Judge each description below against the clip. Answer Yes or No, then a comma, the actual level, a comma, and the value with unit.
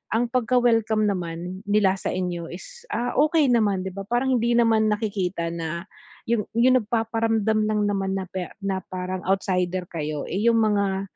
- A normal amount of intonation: Yes, average, 3.7 semitones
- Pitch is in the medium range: No, high, 205 Hz